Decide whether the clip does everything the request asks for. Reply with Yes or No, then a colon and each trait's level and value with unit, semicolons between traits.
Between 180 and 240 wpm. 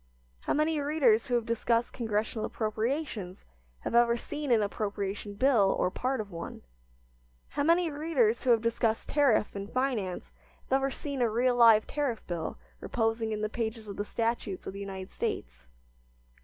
No: average, 170 wpm